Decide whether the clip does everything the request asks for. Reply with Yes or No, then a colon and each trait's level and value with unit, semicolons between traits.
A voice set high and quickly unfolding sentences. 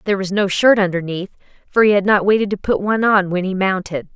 Yes: high, 195 Hz; fast, 245 wpm